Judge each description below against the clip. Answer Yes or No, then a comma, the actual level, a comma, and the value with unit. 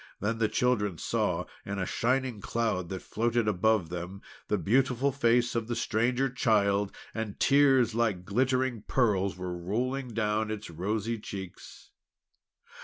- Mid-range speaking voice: No, low, 110 Hz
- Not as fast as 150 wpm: Yes, average, 140 wpm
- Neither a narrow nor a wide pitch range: Yes, average, 3.6 semitones